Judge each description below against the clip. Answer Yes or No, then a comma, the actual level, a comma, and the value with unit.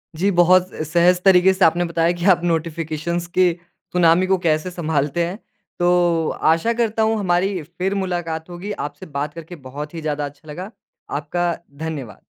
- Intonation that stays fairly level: Yes, narrow, 2.3 semitones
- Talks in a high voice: No, medium, 175 Hz